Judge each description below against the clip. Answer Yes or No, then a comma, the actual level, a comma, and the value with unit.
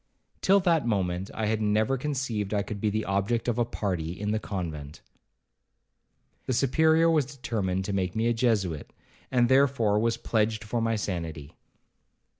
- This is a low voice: Yes, low, 110 Hz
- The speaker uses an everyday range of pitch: Yes, average, 3.8 semitones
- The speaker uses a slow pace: No, average, 165 wpm